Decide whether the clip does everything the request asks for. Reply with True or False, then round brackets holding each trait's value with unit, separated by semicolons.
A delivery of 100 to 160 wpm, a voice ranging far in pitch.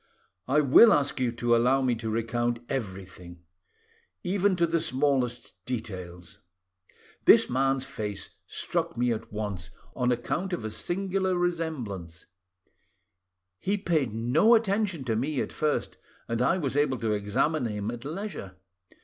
True (140 wpm; 6.6 semitones)